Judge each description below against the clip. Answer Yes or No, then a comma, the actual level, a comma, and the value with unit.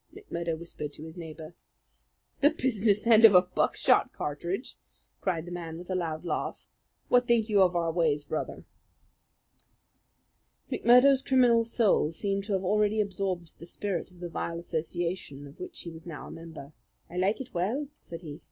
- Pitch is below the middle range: No, medium, 180 Hz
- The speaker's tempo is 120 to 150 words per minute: No, average, 170 wpm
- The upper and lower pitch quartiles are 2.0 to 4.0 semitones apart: No, average, 4.6 semitones